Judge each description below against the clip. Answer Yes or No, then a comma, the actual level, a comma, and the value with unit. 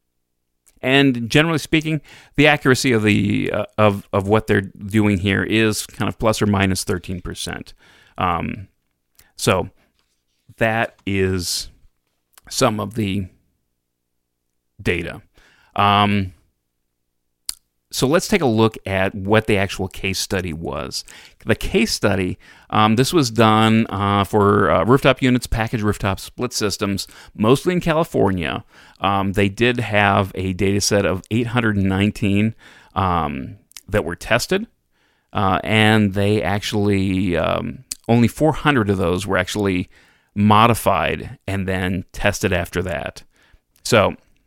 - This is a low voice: Yes, low, 100 Hz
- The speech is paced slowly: Yes, slow, 125 wpm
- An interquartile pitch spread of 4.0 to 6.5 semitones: No, average, 3.4 semitones